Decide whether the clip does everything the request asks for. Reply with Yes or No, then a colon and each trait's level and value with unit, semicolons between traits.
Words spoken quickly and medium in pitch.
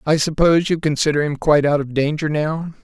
Yes: fast, 210 wpm; medium, 150 Hz